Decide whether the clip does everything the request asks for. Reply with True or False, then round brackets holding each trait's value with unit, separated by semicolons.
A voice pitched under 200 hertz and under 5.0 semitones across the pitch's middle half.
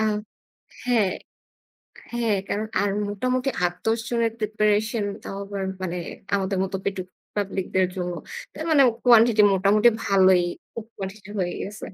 False (205 Hz; 2.8 semitones)